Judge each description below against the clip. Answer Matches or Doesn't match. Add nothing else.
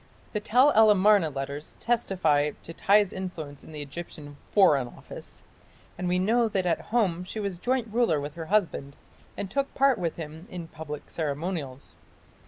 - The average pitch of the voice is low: Doesn't match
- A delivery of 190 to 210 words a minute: Doesn't match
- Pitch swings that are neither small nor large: Doesn't match